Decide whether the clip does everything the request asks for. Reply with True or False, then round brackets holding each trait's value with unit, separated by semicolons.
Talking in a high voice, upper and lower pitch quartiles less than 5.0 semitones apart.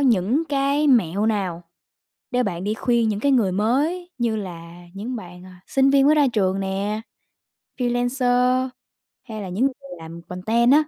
False (225 Hz; 5.3 semitones)